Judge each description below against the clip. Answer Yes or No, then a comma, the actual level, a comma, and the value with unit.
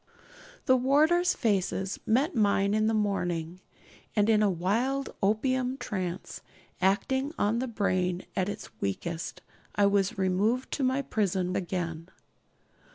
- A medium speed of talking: No, slow, 130 wpm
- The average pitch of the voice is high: Yes, high, 205 Hz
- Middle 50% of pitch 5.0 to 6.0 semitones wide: Yes, wide, 5.5 semitones